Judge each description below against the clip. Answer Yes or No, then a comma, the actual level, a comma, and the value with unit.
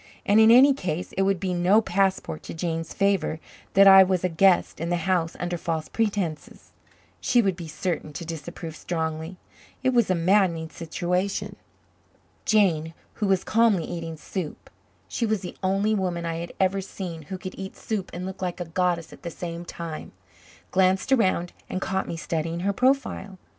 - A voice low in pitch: No, medium, 180 Hz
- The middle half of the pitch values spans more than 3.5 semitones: No, average, 2.8 semitones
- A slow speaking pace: No, average, 180 wpm